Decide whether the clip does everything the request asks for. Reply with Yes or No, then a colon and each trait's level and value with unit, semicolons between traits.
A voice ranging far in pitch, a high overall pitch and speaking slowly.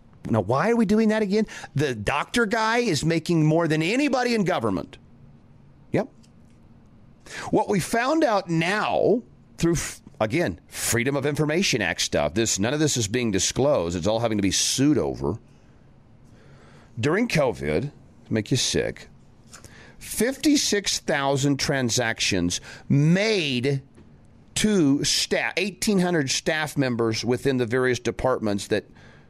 No: wide, 8.5 semitones; medium, 140 Hz; slow, 125 wpm